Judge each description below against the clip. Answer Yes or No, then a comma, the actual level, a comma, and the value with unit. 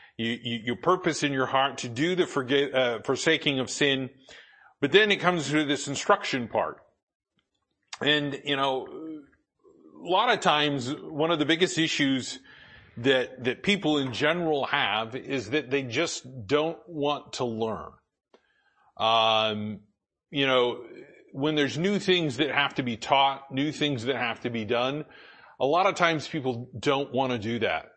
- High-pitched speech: No, medium, 140 Hz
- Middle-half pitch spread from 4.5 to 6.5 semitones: No, average, 3.4 semitones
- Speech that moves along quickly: No, average, 165 wpm